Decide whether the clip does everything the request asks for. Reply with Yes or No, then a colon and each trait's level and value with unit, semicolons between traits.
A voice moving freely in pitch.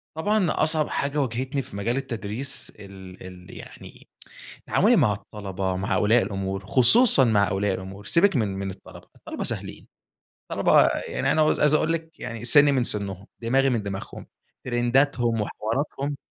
Yes: wide, 6.0 semitones